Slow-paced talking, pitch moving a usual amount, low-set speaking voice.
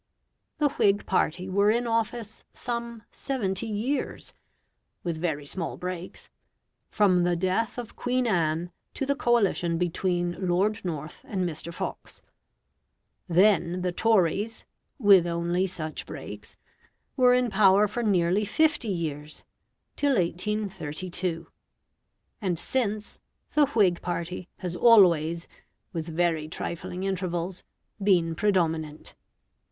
No: slow, 115 wpm; average, 4.0 semitones; medium, 185 Hz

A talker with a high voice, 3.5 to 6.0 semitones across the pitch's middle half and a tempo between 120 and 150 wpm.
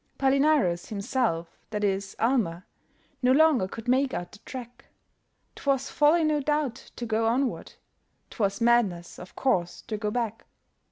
Yes: high, 235 Hz; average, 5.2 semitones; average, 145 wpm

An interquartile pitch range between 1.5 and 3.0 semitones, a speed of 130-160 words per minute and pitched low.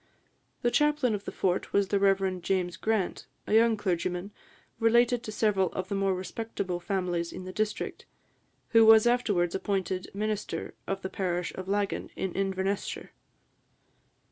No: average, 2.7 semitones; average, 155 wpm; high, 195 Hz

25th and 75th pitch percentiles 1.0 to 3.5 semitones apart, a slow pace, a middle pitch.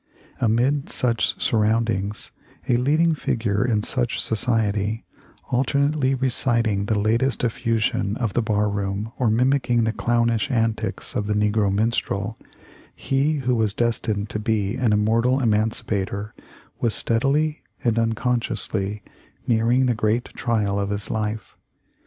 No: average, 2.8 semitones; slow, 130 wpm; low, 115 Hz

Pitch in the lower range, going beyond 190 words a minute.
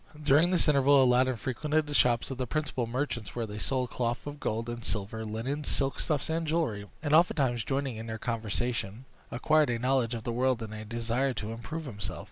Yes: low, 125 Hz; fast, 205 wpm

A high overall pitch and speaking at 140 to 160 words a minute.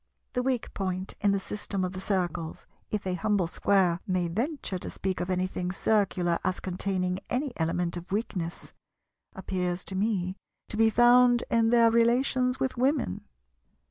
Yes: high, 195 Hz; average, 150 wpm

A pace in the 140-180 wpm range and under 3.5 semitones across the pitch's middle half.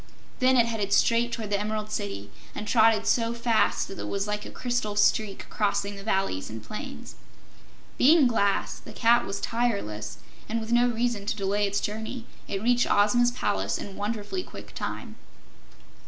Yes: average, 170 wpm; average, 2.7 semitones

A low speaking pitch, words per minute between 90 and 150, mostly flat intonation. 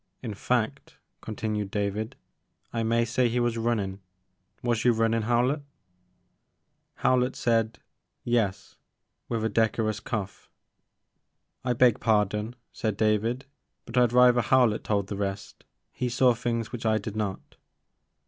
Yes: low, 115 Hz; average, 140 wpm; narrow, 2.1 semitones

